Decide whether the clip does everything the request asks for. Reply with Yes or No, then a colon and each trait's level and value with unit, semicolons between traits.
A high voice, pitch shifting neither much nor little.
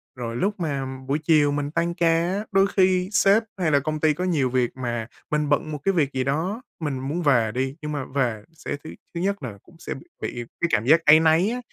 No: medium, 150 Hz; average, 4.6 semitones